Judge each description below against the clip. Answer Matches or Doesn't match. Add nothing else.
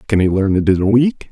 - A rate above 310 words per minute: Matches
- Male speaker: Matches